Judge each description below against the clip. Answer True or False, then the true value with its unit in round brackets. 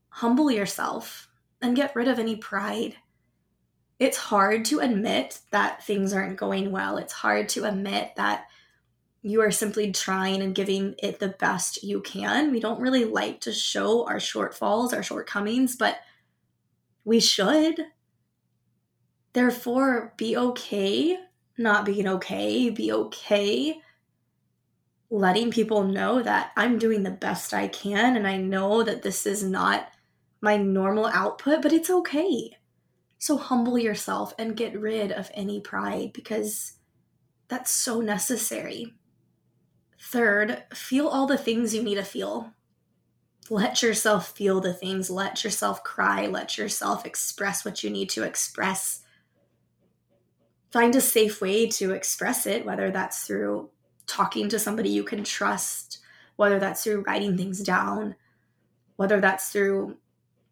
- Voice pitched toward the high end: True (210 Hz)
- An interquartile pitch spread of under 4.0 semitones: True (3.4 semitones)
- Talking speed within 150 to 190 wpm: False (140 wpm)